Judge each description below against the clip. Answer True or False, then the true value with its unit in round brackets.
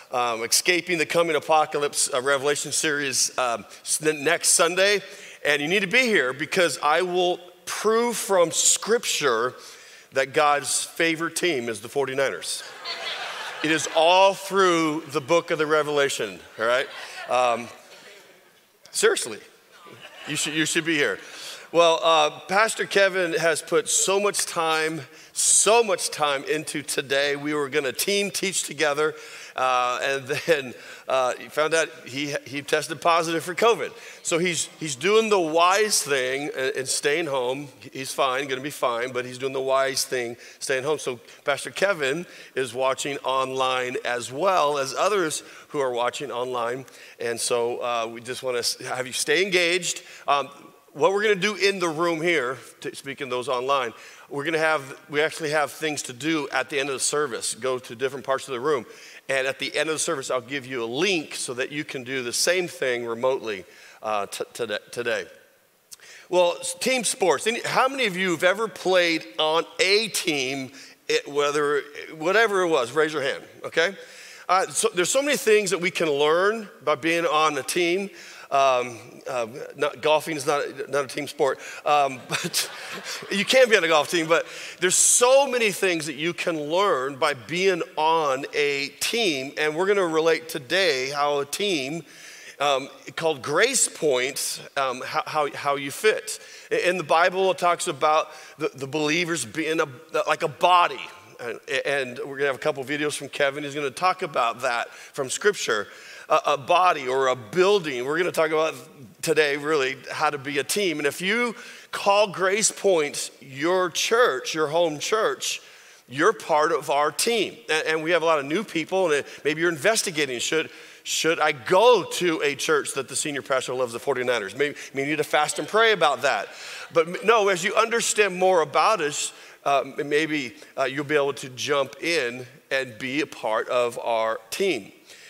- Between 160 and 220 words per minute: True (180 wpm)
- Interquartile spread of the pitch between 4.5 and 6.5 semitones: True (5.1 semitones)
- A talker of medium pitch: True (160 Hz)